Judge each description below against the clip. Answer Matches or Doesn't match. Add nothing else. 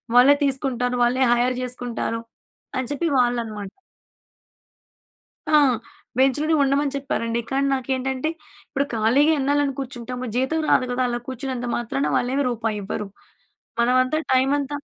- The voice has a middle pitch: Doesn't match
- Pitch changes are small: Matches